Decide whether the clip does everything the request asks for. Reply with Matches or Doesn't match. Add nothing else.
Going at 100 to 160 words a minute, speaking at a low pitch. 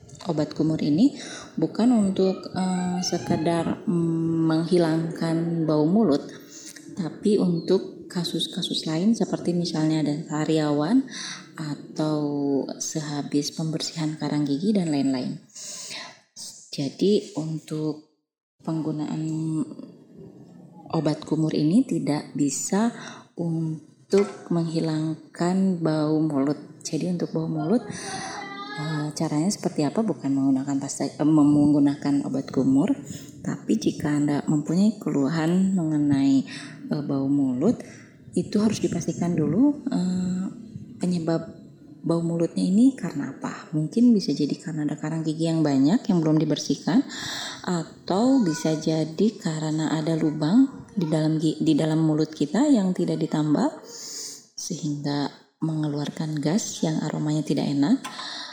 Doesn't match